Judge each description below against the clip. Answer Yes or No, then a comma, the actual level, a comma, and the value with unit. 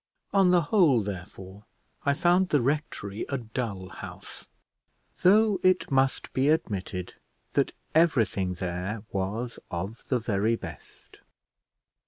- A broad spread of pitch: Yes, wide, 8.1 semitones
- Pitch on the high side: No, low, 115 Hz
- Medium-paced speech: No, slow, 120 wpm